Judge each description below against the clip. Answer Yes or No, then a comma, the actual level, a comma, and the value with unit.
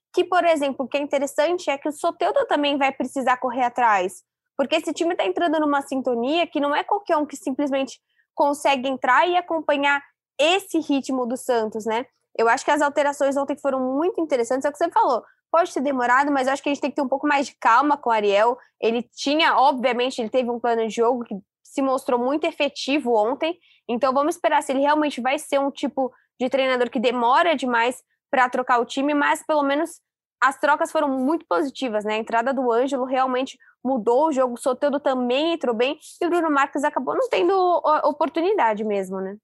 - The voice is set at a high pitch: Yes, very high, 280 Hz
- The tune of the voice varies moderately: Yes, average, 3.4 semitones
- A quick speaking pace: Yes, fast, 210 wpm